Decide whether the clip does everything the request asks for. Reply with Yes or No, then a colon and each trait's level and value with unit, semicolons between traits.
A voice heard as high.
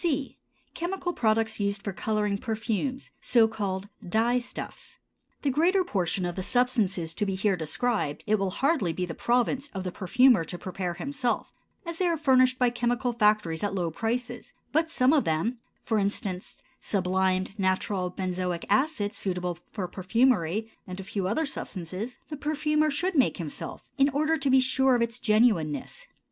Yes: high, 220 Hz